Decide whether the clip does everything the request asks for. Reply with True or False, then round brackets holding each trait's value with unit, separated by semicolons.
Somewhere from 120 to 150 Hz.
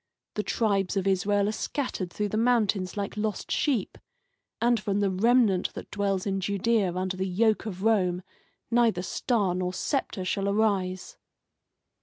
False (200 Hz)